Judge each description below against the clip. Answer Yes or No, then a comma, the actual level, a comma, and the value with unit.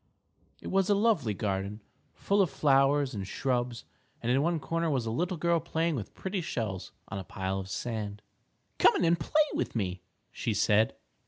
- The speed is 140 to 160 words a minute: No, average, 190 wpm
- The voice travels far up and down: Yes, wide, 8.2 semitones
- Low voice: Yes, low, 130 Hz